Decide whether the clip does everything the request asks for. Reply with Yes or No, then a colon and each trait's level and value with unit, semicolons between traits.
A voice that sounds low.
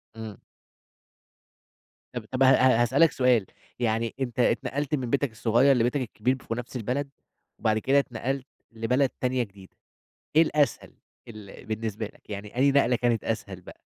Yes: low, 120 Hz